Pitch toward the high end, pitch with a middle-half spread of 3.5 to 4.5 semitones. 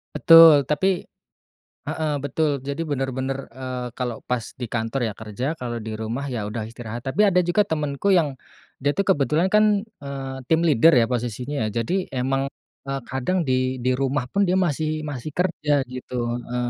No: low, 135 Hz; average, 3.8 semitones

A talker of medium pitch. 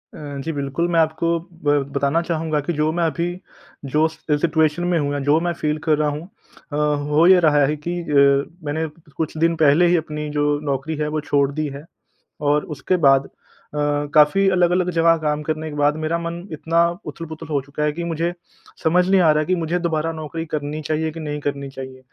Yes: medium, 155 Hz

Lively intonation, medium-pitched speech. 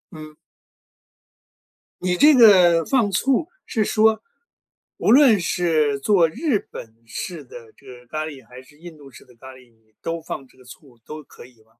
Yes: wide, 8.3 semitones; medium, 160 Hz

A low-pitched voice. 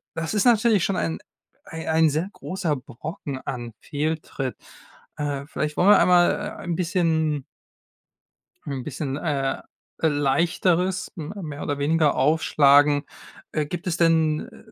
No: medium, 155 Hz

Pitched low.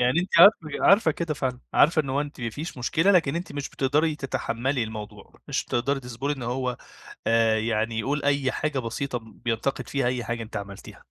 Yes: low, 130 Hz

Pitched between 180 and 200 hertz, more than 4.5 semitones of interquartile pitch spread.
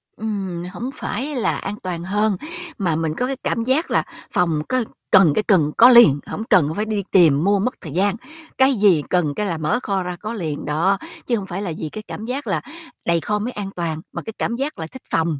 Yes: high, 195 Hz; average, 5.0 semitones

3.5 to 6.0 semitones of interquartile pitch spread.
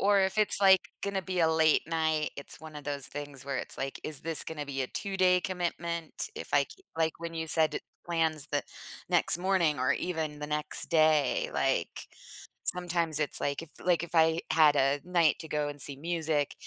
No: average, 2.7 semitones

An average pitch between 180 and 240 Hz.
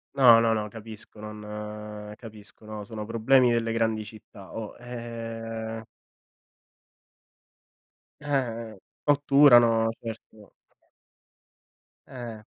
No: low, 115 Hz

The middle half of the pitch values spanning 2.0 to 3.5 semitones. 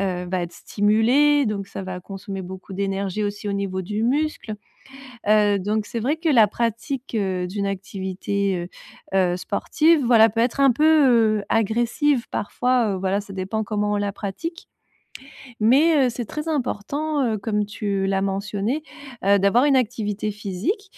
No: average, 4.0 semitones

